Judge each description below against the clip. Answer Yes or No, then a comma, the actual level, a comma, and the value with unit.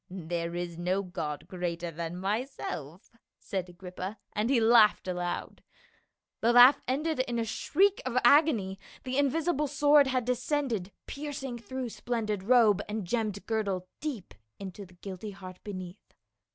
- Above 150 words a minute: No, average, 145 wpm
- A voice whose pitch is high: Yes, high, 215 Hz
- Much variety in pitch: Yes, wide, 5.8 semitones